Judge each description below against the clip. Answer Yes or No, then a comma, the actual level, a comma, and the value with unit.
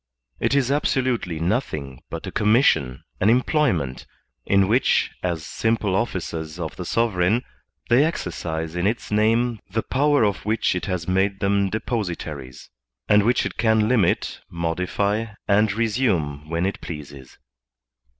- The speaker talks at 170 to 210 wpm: No, average, 140 wpm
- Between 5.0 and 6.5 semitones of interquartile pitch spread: Yes, average, 5.3 semitones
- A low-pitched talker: Yes, low, 100 Hz